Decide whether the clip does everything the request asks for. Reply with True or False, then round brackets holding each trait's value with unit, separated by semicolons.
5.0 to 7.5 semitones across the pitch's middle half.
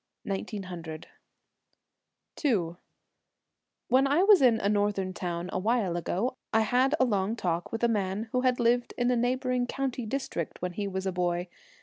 True (5.3 semitones)